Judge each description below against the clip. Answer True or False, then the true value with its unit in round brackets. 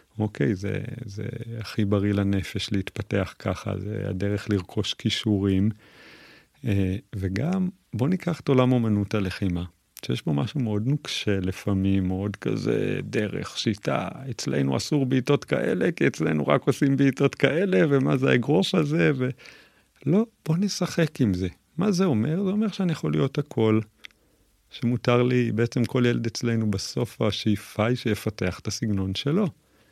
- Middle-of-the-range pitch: False (110 Hz)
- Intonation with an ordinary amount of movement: False (5.7 semitones)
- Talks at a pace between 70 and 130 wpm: False (145 wpm)